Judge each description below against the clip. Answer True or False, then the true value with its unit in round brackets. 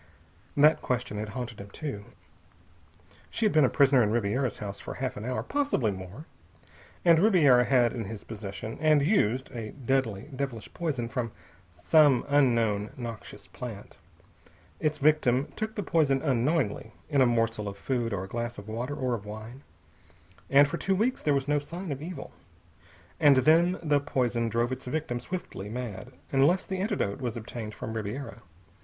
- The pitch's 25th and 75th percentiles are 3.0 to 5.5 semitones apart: True (4.7 semitones)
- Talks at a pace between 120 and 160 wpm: False (170 wpm)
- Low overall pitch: True (125 Hz)